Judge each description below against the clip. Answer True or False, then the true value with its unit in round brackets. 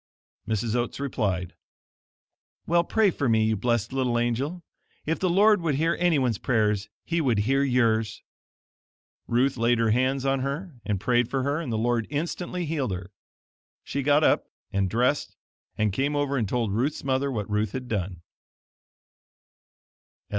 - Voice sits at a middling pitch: False (125 Hz)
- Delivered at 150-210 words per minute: True (160 wpm)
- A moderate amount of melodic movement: True (4.5 semitones)